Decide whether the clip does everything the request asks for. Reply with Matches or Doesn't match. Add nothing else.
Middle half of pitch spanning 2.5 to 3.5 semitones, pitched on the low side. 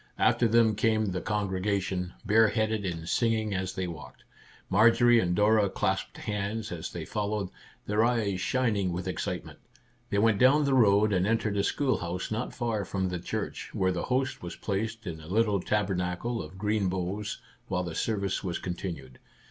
Matches